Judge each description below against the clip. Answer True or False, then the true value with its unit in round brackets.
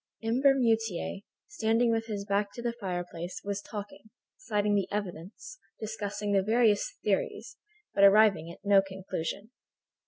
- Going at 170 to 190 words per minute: False (135 wpm)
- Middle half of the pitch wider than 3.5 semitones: False (2.5 semitones)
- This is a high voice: True (205 Hz)